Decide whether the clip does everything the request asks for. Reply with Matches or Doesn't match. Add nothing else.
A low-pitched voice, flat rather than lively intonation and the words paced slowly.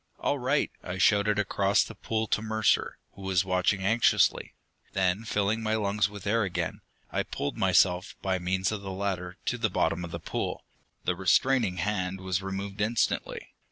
Doesn't match